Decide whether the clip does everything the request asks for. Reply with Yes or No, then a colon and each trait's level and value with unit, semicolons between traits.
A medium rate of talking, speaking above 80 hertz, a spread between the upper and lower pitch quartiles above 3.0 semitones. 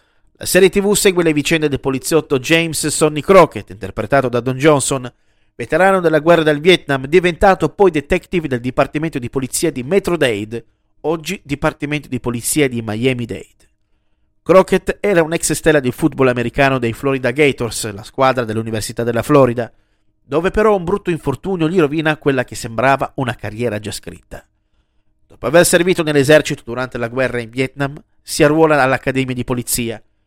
Yes: average, 160 wpm; medium, 140 Hz; average, 5.1 semitones